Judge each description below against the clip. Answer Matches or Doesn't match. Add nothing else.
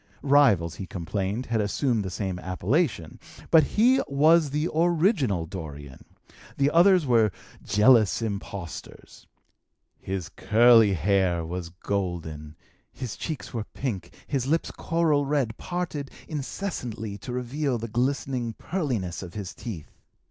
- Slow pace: Matches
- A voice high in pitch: Doesn't match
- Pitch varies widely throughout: Matches